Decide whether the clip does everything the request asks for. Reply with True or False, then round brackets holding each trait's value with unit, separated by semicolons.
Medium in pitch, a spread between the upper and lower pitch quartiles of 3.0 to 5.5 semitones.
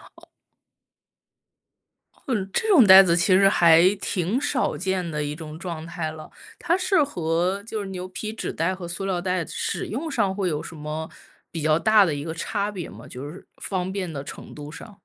True (180 Hz; 3.8 semitones)